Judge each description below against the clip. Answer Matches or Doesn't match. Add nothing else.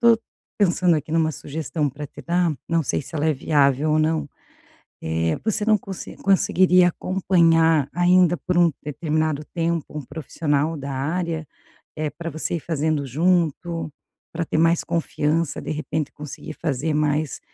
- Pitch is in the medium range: Matches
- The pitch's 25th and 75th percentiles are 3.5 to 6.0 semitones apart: Doesn't match